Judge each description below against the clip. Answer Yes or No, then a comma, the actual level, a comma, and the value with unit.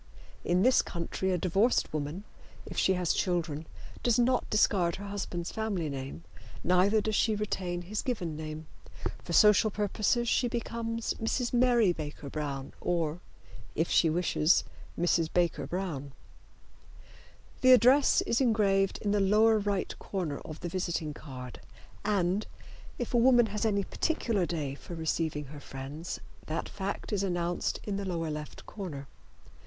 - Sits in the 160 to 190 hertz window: Yes, medium, 185 Hz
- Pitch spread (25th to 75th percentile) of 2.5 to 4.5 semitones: No, average, 5.0 semitones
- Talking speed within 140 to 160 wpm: Yes, average, 150 wpm